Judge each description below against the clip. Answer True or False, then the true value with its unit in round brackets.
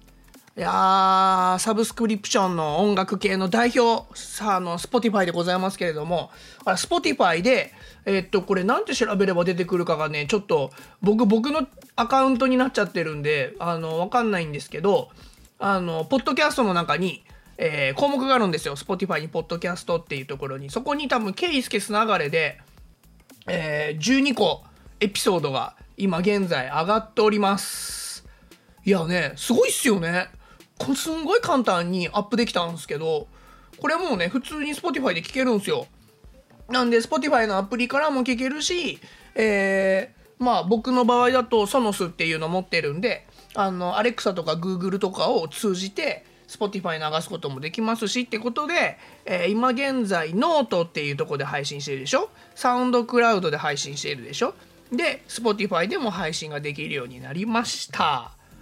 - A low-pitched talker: False (205 Hz)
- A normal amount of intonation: False (6.3 semitones)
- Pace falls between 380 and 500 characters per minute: True (395 characters per minute)